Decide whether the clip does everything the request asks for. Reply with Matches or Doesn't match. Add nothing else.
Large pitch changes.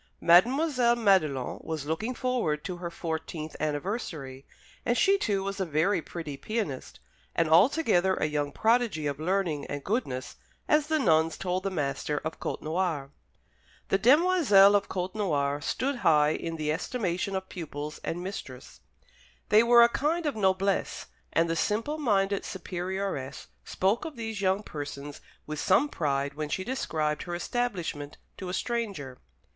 Matches